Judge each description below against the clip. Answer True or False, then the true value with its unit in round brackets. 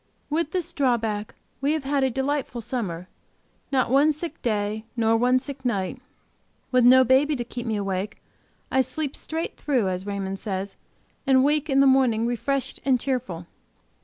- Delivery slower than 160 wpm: False (165 wpm)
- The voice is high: True (255 Hz)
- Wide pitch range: False (4.2 semitones)